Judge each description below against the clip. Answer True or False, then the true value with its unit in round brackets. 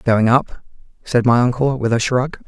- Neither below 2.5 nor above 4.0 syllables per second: False (4.4 syllables/s)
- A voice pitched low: True (125 Hz)